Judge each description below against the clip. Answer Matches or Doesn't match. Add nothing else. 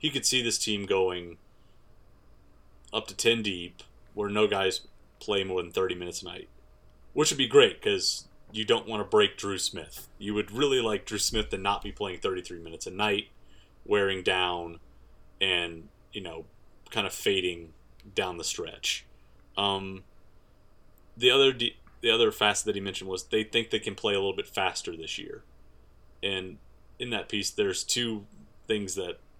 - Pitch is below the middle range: Matches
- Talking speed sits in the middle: Matches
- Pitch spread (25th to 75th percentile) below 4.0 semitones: Doesn't match